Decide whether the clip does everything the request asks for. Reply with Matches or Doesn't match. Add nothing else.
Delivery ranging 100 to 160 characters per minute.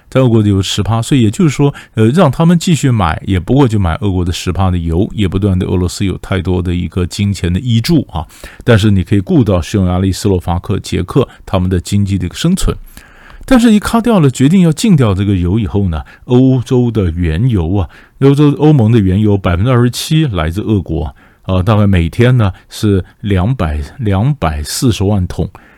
Doesn't match